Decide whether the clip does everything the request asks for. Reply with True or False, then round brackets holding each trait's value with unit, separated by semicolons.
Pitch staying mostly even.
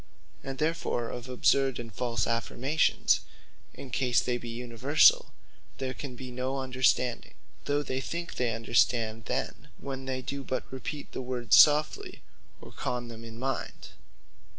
True (2.1 semitones)